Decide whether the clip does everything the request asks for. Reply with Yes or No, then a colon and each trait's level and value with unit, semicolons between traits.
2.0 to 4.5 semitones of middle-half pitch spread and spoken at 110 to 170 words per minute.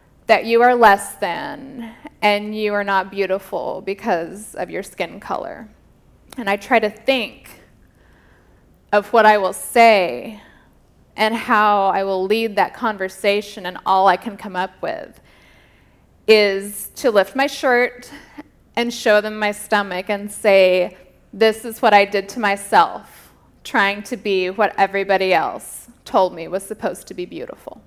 Yes: narrow, 2.6 semitones; average, 155 wpm